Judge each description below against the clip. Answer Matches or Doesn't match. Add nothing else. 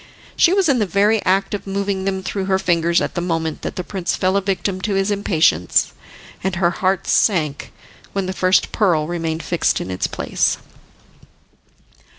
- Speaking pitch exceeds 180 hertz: Matches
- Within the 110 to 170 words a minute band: Doesn't match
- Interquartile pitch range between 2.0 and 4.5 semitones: Matches